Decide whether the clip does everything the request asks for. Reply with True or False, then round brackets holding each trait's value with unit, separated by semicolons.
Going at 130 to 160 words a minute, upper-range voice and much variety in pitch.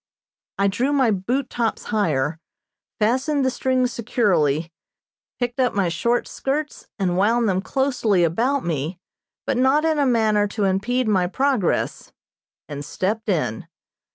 True (140 wpm; 220 Hz; 5.7 semitones)